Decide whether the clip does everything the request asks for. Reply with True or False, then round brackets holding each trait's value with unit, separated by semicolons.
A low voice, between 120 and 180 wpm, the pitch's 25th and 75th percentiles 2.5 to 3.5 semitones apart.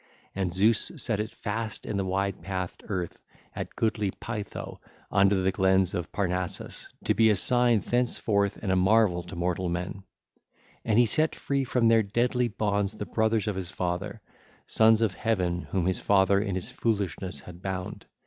True (100 Hz; 175 wpm; 3.1 semitones)